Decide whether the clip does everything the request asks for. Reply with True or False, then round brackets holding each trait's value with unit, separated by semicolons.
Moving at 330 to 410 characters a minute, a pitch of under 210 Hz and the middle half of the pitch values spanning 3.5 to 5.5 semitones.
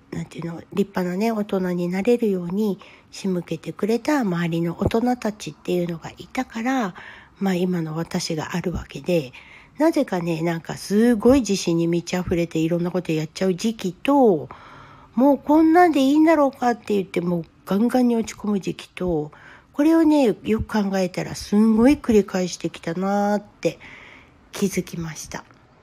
True (350 characters per minute; 190 Hz; 5.2 semitones)